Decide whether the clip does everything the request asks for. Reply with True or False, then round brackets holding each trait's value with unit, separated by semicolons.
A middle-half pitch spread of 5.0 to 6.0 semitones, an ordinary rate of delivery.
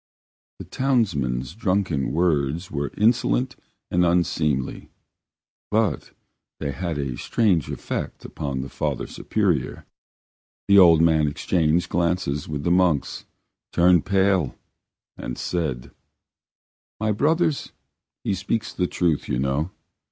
False (5.3 semitones; 115 wpm)